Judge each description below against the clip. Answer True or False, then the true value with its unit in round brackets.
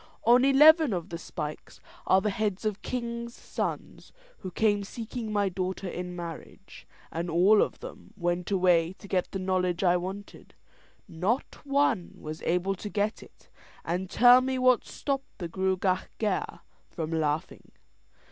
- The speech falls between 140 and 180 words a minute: True (155 wpm)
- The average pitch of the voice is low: False (190 Hz)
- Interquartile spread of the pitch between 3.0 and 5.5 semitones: True (4.5 semitones)